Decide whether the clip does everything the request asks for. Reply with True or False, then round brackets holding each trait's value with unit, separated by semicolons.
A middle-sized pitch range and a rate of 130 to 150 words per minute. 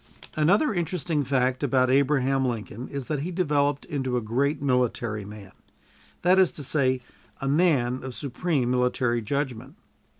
True (3.1 semitones; 145 wpm)